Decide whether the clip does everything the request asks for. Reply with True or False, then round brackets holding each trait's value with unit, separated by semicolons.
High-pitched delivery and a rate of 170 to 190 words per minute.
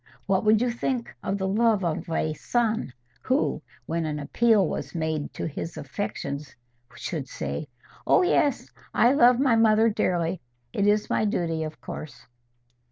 False (200 Hz; 160 wpm)